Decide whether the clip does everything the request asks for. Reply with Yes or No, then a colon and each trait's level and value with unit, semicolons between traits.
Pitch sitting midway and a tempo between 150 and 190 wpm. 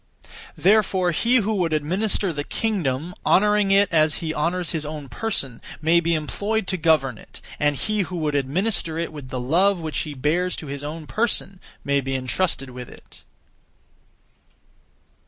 Yes: medium, 165 Hz; average, 165 wpm